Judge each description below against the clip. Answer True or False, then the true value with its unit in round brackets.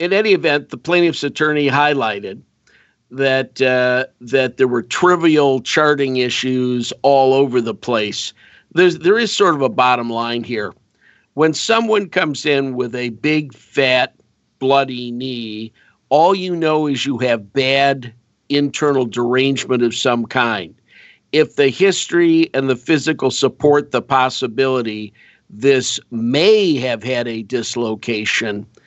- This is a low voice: True (130 Hz)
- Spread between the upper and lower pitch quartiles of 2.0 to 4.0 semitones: True (3.4 semitones)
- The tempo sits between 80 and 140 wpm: True (135 wpm)